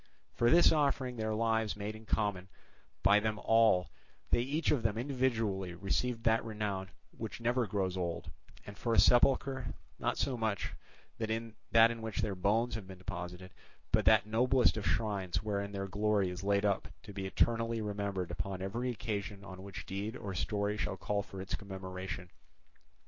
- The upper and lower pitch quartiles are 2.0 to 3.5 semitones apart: Yes, average, 2.9 semitones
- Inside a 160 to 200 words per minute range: Yes, average, 175 wpm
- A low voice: Yes, low, 105 Hz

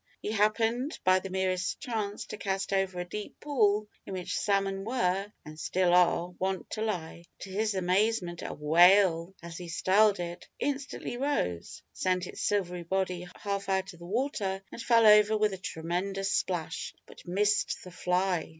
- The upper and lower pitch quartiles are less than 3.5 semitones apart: Yes, average, 2.8 semitones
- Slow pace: No, average, 170 wpm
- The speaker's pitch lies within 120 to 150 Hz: No, high, 190 Hz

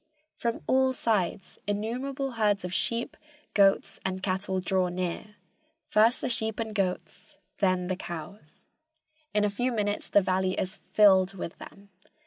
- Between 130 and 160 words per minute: Yes, average, 145 wpm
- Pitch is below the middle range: No, high, 200 Hz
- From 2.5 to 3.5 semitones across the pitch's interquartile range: Yes, average, 3.0 semitones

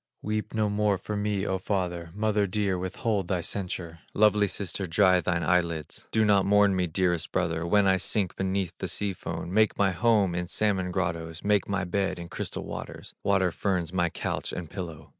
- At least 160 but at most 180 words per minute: No, average, 190 wpm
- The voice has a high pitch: No, very low, 95 Hz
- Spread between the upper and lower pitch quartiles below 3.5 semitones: Yes, average, 2.8 semitones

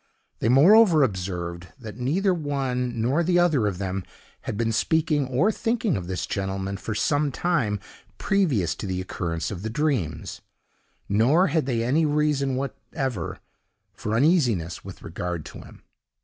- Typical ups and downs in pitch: No, wide, 7.7 semitones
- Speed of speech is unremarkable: Yes, average, 150 wpm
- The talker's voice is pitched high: No, low, 125 Hz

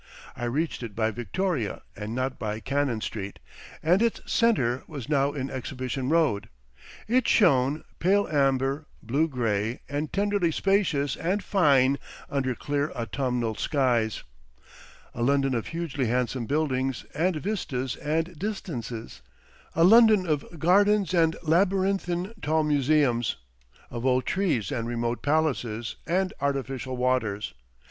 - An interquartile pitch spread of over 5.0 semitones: Yes, wide, 5.5 semitones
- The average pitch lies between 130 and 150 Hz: Yes, medium, 140 Hz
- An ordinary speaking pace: No, slow, 130 wpm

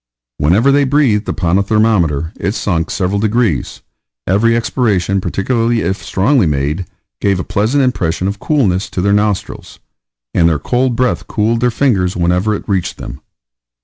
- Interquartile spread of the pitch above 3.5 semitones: Yes, average, 4.4 semitones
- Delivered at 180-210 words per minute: No, average, 155 wpm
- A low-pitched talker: Yes, low, 100 Hz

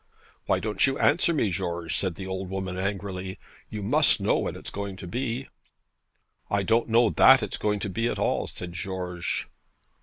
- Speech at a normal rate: Yes, average, 185 wpm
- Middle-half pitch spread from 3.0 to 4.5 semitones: Yes, average, 3.4 semitones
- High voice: No, low, 100 Hz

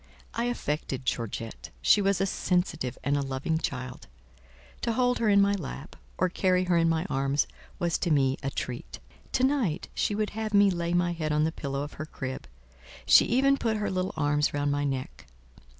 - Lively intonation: Yes, wide, 6.2 semitones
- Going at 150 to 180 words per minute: No, average, 195 wpm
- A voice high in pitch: No, medium, 165 Hz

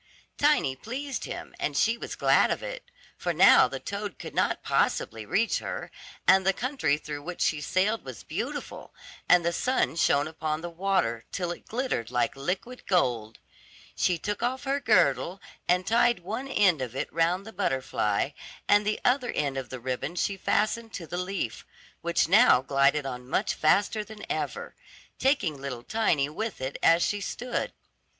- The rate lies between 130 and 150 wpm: No, average, 175 wpm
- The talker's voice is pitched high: No, medium, 180 Hz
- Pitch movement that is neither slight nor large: No, wide, 7.7 semitones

